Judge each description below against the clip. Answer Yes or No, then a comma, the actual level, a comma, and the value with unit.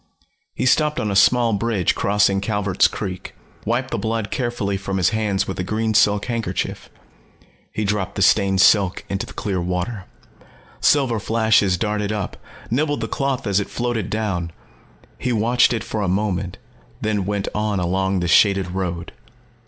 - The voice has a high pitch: No, low, 105 Hz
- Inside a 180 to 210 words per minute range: No, average, 165 wpm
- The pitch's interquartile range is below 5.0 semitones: Yes, average, 2.8 semitones